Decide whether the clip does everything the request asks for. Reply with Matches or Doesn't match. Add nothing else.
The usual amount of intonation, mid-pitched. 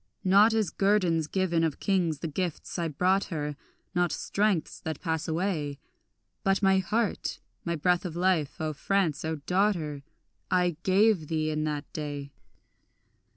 Matches